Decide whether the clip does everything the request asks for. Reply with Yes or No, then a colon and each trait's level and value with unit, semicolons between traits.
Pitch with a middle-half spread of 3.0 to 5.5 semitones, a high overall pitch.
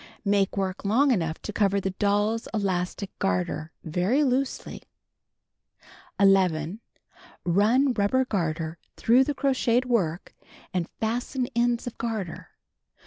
Yes: average, 5.2 semitones; high, 205 Hz